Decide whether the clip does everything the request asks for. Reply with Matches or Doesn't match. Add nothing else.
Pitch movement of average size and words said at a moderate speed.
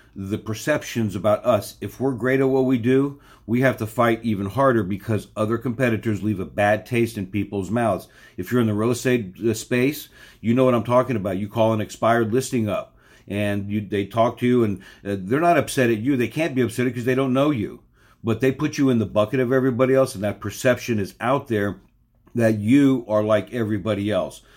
Doesn't match